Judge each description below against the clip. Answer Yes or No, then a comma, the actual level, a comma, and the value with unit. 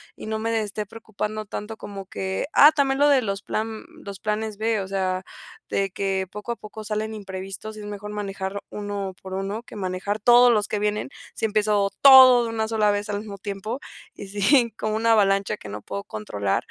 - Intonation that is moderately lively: No, narrow, 2.0 semitones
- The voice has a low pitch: No, high, 210 Hz